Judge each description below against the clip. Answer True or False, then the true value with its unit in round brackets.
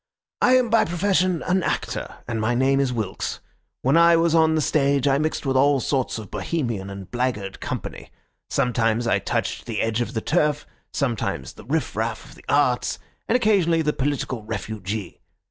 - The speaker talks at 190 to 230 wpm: False (180 wpm)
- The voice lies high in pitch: False (135 Hz)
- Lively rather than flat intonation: True (6.1 semitones)